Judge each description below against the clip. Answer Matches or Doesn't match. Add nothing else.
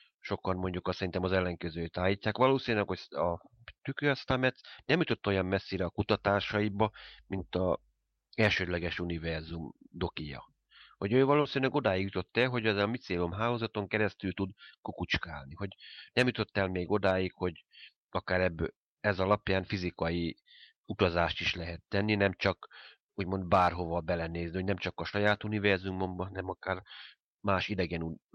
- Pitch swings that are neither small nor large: Matches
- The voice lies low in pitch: Matches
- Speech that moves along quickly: Doesn't match